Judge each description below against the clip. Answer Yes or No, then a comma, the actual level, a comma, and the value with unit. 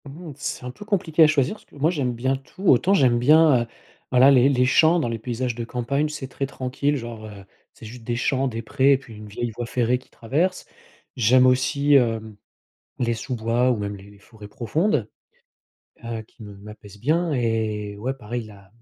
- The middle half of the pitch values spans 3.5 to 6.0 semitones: Yes, average, 3.8 semitones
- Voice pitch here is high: No, low, 125 Hz